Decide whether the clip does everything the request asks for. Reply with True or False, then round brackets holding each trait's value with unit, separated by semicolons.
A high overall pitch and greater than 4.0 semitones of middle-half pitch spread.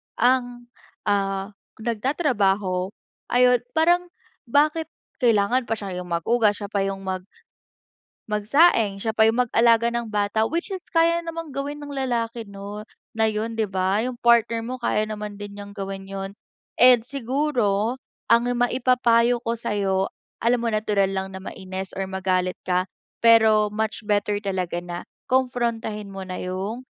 False (220 Hz; 3.7 semitones)